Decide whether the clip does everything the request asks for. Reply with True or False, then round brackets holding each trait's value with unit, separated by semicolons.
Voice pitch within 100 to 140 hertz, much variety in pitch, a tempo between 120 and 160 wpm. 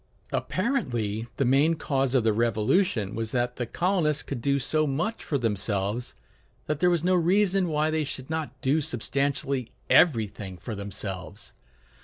True (135 Hz; 5.9 semitones; 155 wpm)